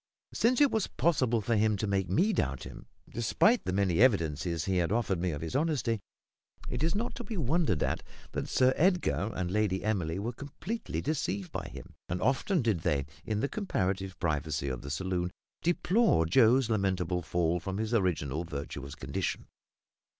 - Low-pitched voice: Yes, low, 100 Hz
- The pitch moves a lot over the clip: Yes, wide, 7.5 semitones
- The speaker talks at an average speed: Yes, average, 180 wpm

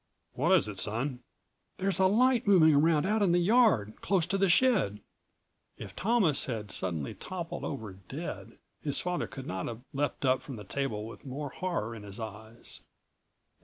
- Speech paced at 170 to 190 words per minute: Yes, average, 175 wpm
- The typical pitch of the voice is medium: Yes, medium, 145 Hz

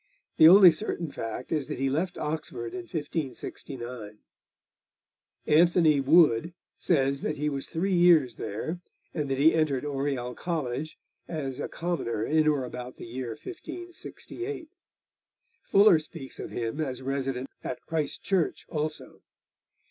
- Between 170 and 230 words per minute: No, average, 140 wpm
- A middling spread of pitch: Yes, average, 4.3 semitones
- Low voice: No, medium, 150 Hz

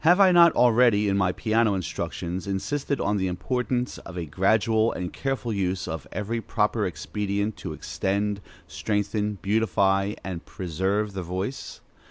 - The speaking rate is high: No, average, 150 wpm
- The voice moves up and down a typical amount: Yes, average, 3.2 semitones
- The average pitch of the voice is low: Yes, low, 105 Hz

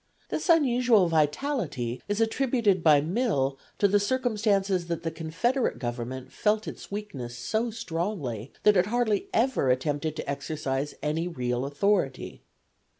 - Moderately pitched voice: Yes, medium, 175 Hz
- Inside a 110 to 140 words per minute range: Yes, slow, 135 wpm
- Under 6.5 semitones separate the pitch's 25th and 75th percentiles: No, wide, 7.5 semitones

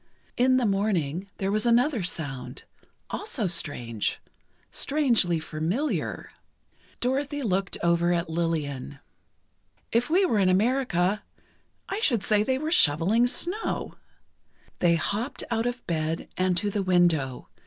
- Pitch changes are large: Yes, wide, 6.5 semitones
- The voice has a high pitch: Yes, high, 195 Hz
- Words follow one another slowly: Yes, slow, 120 wpm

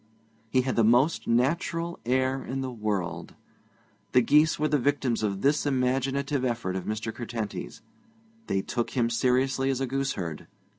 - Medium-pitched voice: No, low, 130 Hz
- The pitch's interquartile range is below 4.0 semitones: Yes, average, 2.9 semitones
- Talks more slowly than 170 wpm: Yes, average, 155 wpm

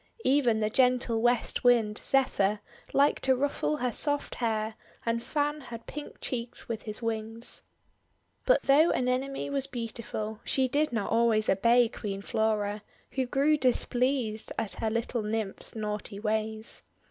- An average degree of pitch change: Yes, average, 3.3 semitones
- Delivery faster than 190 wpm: No, average, 145 wpm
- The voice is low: No, high, 235 Hz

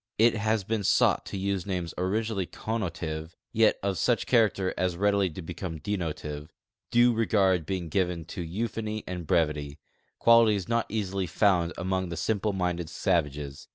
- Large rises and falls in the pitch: No, average, 3.9 semitones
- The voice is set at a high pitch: No, very low, 95 Hz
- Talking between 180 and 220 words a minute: No, average, 160 wpm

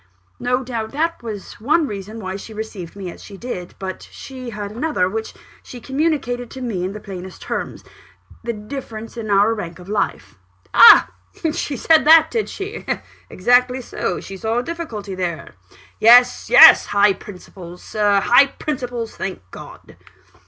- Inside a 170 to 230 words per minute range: No, average, 160 wpm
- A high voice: Yes, high, 220 Hz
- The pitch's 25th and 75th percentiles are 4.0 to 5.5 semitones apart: Yes, average, 4.4 semitones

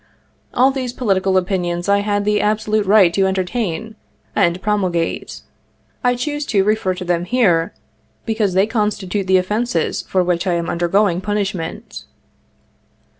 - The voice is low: No, high, 195 Hz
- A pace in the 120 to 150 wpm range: Yes, average, 145 wpm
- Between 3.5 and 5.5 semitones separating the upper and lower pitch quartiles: No, average, 3.1 semitones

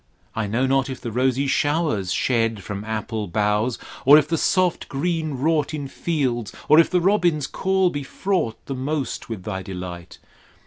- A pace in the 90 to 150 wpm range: No, average, 175 wpm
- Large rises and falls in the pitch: Yes, wide, 6.0 semitones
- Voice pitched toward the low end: Yes, low, 130 Hz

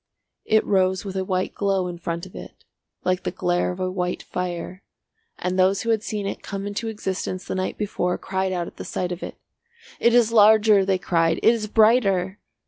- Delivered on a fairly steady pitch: Yes, narrow, 2.3 semitones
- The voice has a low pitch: No, high, 190 Hz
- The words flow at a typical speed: No, fast, 210 wpm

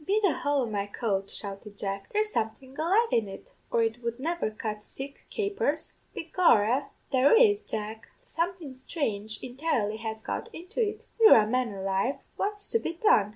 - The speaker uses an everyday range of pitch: No, wide, 8.2 semitones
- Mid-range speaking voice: No, very high, 255 Hz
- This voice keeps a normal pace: Yes, average, 175 wpm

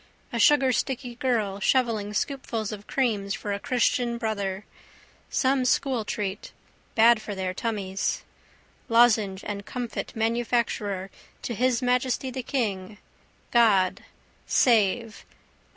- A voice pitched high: Yes, high, 230 Hz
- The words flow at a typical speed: No, slow, 110 wpm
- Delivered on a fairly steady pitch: No, average, 3.5 semitones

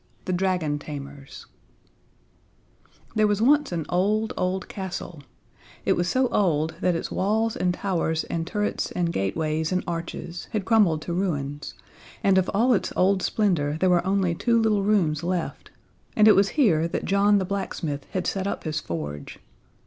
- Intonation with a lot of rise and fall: No, average, 3.9 semitones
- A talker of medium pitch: Yes, medium, 180 Hz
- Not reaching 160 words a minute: No, average, 165 wpm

